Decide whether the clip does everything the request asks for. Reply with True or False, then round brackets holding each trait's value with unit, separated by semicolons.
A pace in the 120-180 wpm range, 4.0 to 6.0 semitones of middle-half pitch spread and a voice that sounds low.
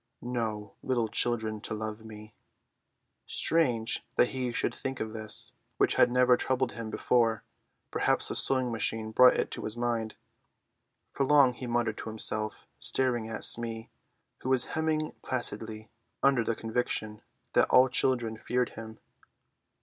False (150 wpm; 2.5 semitones; 115 Hz)